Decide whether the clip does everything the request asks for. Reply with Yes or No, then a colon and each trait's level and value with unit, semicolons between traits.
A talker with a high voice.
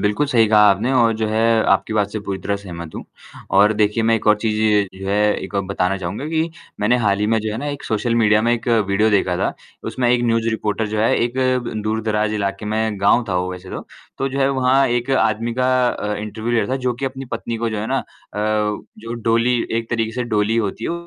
No: low, 110 Hz